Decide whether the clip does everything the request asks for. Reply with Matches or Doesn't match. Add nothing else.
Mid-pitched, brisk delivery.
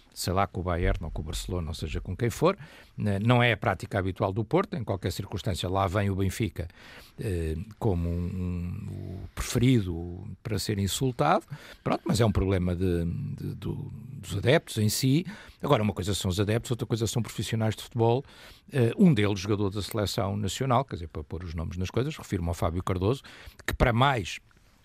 Doesn't match